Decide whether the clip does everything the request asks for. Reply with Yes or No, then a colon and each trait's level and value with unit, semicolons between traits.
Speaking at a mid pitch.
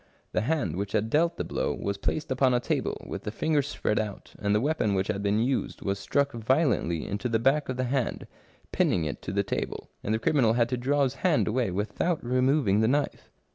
No: low, 120 Hz